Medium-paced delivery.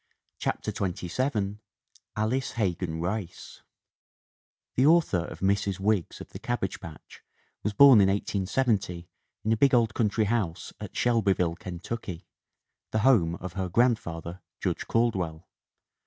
No: slow, 130 wpm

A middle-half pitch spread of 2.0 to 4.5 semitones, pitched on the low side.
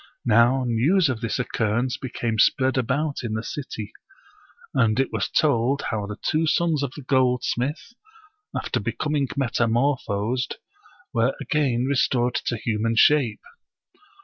Yes: average, 3.5 semitones; low, 125 Hz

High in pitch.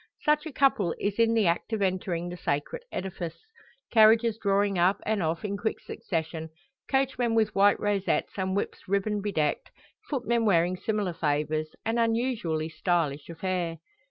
Yes: high, 195 Hz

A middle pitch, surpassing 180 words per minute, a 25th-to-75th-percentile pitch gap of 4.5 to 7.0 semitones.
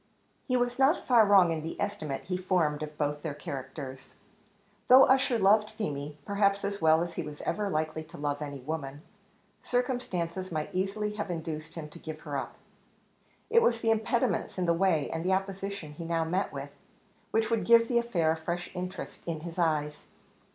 Yes: medium, 175 Hz; average, 190 wpm; average, 5.0 semitones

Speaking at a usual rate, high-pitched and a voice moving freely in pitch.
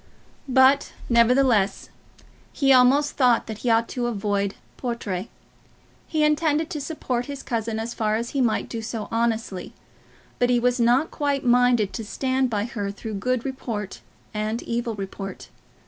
No: average, 155 wpm; high, 235 Hz; average, 3.2 semitones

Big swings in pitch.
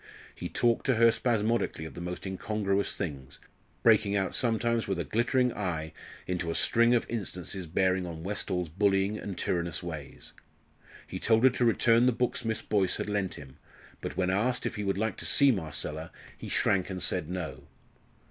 No: average, 4.5 semitones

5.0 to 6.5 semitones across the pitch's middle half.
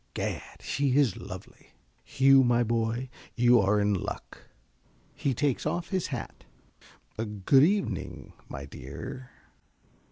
No: average, 4.5 semitones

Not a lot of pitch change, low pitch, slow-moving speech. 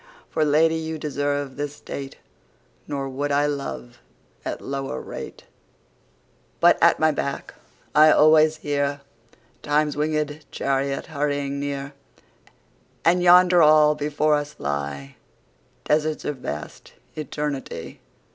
No: narrow, 1.8 semitones; medium, 145 Hz; slow, 100 wpm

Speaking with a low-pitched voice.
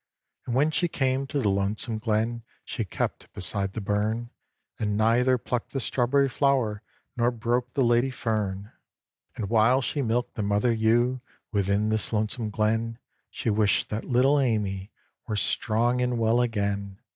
Yes: low, 115 Hz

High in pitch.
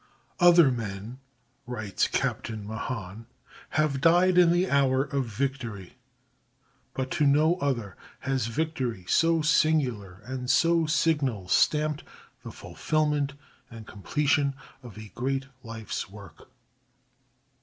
No: low, 135 Hz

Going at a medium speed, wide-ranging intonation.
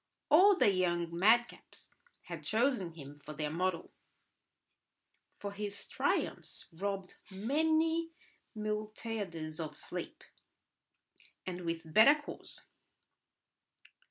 No: slow, 100 wpm; wide, 5.7 semitones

